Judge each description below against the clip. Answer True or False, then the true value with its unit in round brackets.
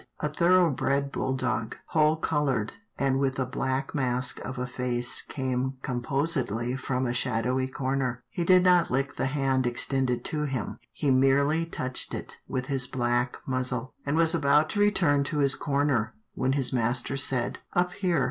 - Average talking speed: True (170 wpm)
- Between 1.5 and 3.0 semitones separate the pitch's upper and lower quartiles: True (2.6 semitones)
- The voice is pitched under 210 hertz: True (135 Hz)